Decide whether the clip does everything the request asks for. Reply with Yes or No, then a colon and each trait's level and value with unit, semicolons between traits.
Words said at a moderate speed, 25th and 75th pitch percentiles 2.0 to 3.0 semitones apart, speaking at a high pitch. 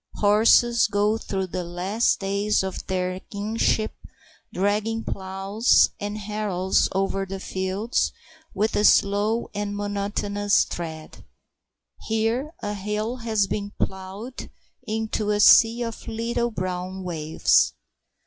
No: slow, 110 wpm; narrow, 2.4 semitones; high, 205 Hz